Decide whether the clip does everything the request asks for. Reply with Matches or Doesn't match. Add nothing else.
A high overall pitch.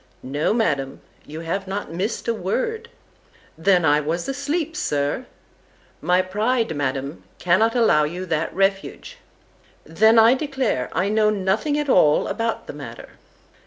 Matches